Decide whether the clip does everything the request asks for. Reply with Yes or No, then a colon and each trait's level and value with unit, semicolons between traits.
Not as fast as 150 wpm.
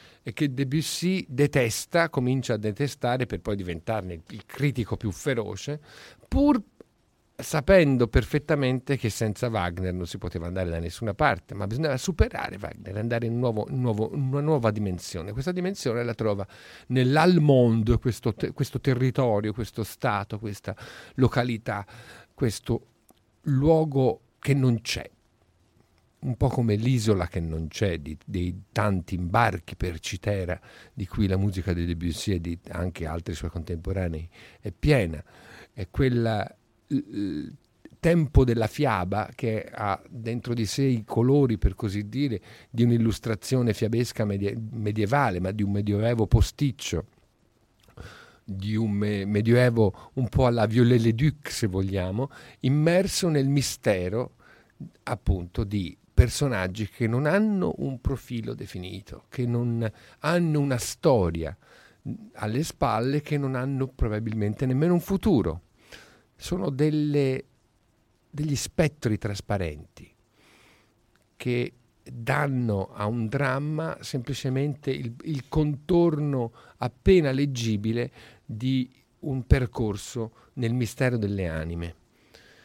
Yes: average, 125 wpm